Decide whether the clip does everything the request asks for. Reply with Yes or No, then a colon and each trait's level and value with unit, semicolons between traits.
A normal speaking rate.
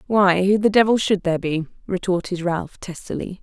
Yes: average, 175 wpm